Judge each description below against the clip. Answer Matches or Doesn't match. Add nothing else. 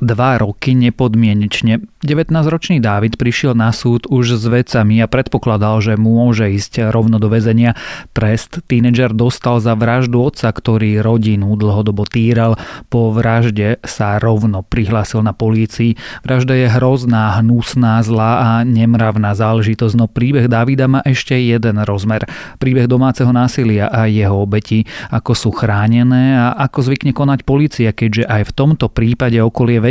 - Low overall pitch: Matches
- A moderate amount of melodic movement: Doesn't match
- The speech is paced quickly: Doesn't match